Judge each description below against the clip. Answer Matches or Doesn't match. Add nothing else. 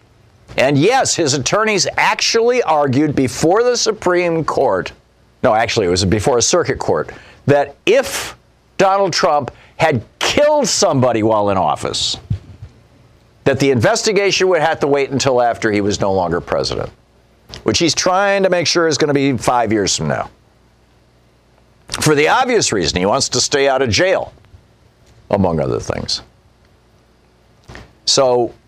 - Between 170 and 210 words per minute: Doesn't match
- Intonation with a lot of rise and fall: Matches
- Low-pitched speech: Matches